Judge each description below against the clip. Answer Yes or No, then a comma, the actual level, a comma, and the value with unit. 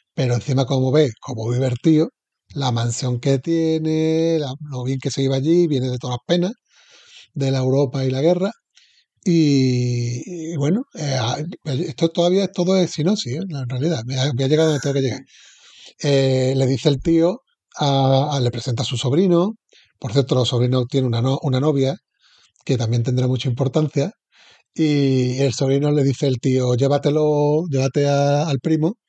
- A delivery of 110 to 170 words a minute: No, average, 180 wpm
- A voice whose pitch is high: No, medium, 140 Hz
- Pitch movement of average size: Yes, average, 3.8 semitones